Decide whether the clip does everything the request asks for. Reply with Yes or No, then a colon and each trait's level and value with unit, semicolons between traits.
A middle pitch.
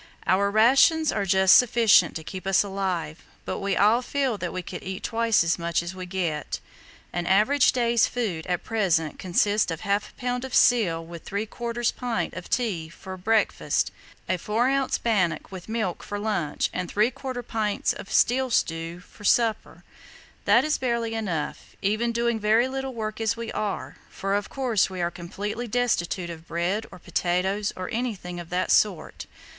No: high, 205 Hz